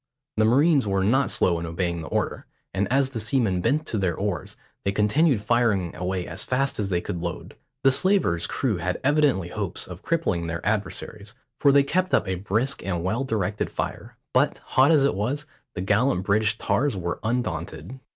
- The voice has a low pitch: Yes, low, 105 Hz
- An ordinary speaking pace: Yes, average, 190 wpm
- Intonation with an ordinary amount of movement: No, wide, 6.6 semitones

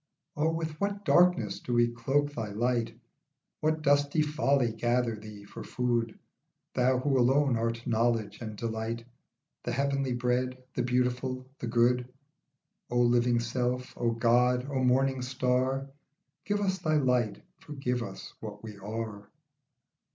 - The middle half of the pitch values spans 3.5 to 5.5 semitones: No, narrow, 2.6 semitones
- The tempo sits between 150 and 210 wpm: No, average, 140 wpm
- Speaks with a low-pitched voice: Yes, low, 125 Hz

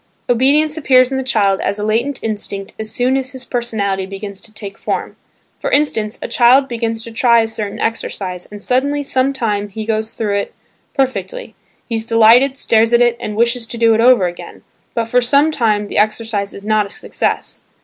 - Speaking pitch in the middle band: No, high, 230 Hz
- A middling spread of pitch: Yes, average, 3.3 semitones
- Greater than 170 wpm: Yes, average, 200 wpm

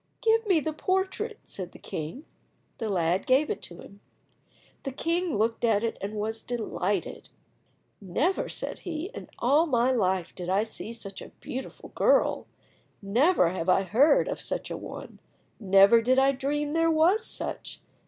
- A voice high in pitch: Yes, high, 240 Hz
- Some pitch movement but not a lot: No, wide, 7.9 semitones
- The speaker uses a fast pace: No, average, 165 wpm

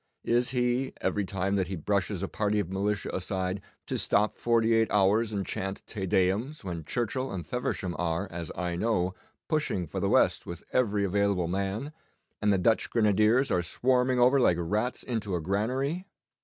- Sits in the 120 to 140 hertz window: No, low, 100 Hz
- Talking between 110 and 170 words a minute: No, average, 180 wpm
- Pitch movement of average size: Yes, average, 4.3 semitones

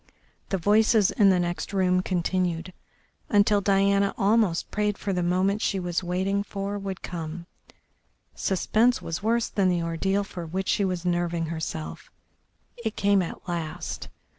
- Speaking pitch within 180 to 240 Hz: Yes, high, 190 Hz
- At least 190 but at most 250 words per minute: No, average, 150 wpm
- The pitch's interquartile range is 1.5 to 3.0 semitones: Yes, narrow, 2.6 semitones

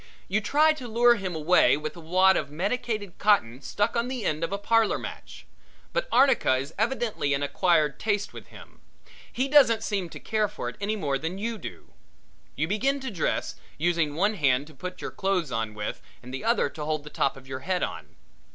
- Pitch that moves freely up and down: Yes, wide, 6.8 semitones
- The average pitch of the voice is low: No, high, 190 Hz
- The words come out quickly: Yes, fast, 210 wpm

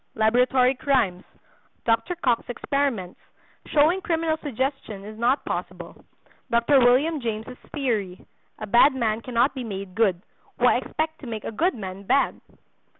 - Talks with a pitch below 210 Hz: No, high, 245 Hz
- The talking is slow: Yes, slow, 125 wpm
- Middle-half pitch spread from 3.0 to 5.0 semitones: Yes, average, 4.5 semitones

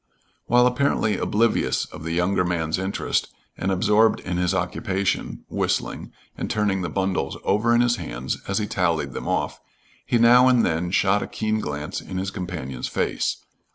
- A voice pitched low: Yes, very low, 95 Hz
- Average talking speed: Yes, average, 170 wpm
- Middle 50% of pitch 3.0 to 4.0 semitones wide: Yes, average, 3.6 semitones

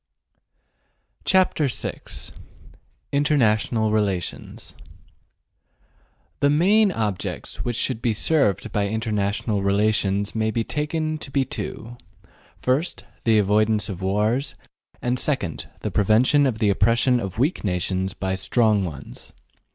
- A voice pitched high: No, low, 110 Hz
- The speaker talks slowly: Yes, slow, 115 wpm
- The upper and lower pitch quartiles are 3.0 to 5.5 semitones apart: Yes, average, 4.8 semitones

